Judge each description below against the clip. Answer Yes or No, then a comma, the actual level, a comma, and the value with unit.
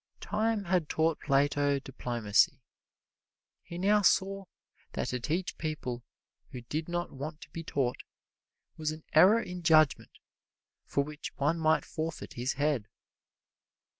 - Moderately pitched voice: Yes, medium, 155 Hz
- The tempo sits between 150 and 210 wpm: No, slow, 135 wpm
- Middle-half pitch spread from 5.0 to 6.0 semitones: No, average, 3.9 semitones